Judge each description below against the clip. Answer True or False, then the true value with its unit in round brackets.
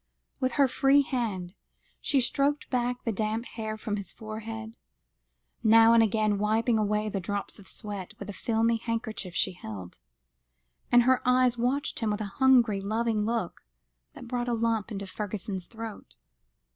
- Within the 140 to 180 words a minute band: True (160 wpm)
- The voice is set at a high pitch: True (225 Hz)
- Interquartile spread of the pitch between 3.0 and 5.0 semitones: False (2.6 semitones)